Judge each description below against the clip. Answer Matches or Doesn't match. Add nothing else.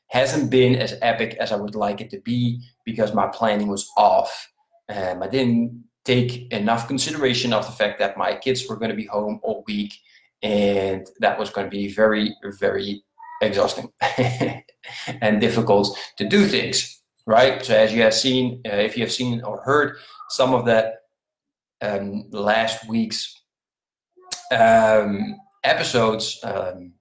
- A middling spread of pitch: Matches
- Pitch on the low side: Matches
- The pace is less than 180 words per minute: Matches